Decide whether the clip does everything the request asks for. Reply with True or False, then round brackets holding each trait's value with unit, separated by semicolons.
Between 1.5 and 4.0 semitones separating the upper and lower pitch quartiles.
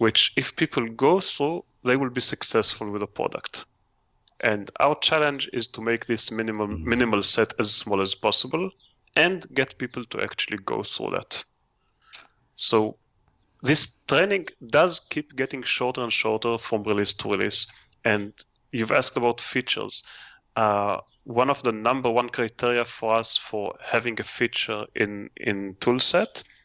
True (2.9 semitones)